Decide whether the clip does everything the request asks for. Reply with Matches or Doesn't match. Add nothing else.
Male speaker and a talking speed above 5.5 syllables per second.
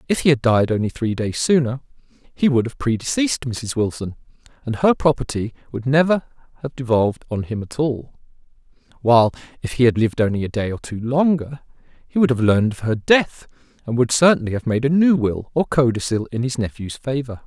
Matches